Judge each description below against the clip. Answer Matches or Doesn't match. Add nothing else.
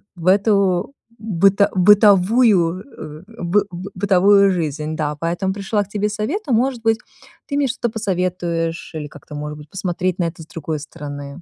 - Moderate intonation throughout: Matches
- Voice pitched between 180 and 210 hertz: Matches